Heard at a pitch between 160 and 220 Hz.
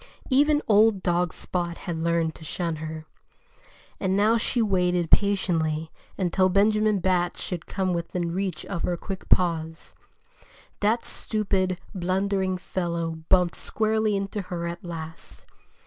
Yes: medium, 185 Hz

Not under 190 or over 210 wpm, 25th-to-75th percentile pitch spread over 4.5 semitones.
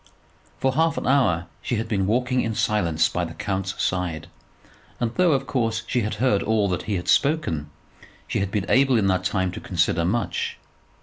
Yes: average, 195 wpm; average, 5.3 semitones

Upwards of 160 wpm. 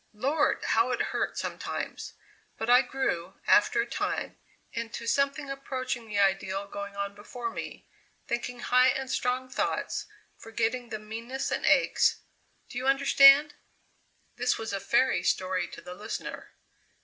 No: average, 145 wpm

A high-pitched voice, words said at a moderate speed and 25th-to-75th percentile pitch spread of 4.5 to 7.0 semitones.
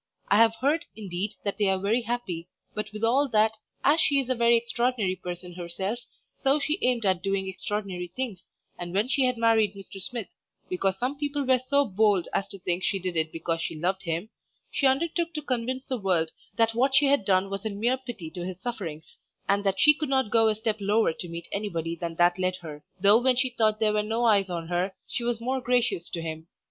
No: high, 210 Hz; fast, 225 wpm; average, 5.1 semitones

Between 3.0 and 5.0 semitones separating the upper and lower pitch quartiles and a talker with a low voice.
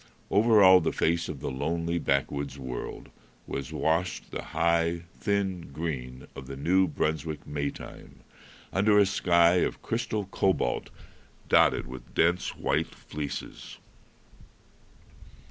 Yes: average, 4.7 semitones; very low, 85 Hz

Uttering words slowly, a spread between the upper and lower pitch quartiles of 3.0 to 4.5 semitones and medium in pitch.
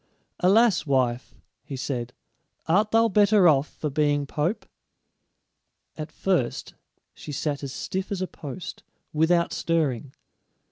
No: slow, 125 wpm; average, 5.1 semitones; medium, 155 Hz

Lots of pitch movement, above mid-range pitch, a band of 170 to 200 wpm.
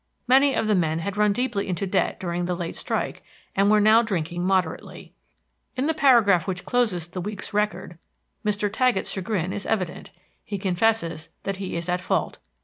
No: average, 3.4 semitones; high, 195 Hz; average, 180 wpm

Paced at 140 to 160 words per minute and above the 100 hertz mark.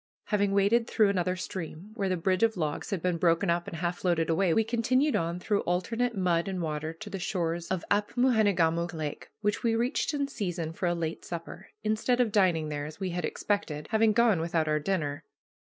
No: fast, 205 wpm; medium, 185 Hz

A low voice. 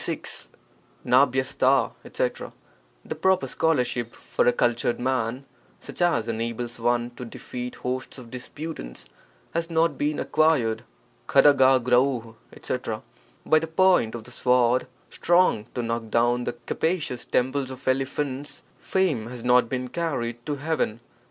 Yes: low, 125 Hz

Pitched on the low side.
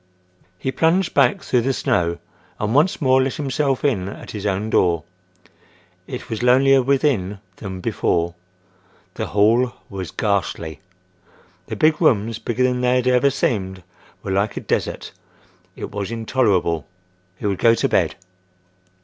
Yes: low, 115 Hz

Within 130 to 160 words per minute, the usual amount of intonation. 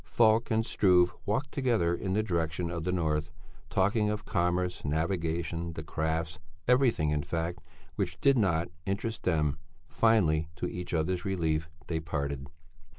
Yes: average, 150 wpm; average, 4.4 semitones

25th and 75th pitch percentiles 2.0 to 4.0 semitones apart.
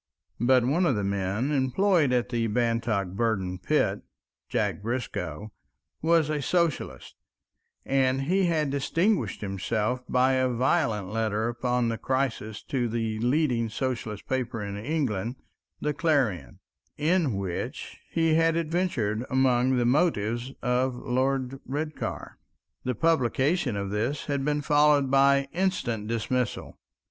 No: average, 4.6 semitones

